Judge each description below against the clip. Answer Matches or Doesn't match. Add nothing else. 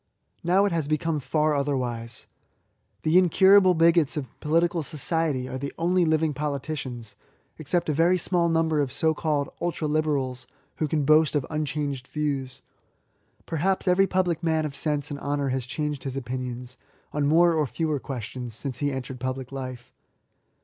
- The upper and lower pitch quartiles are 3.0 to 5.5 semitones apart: Matches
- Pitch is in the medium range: Matches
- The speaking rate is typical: Matches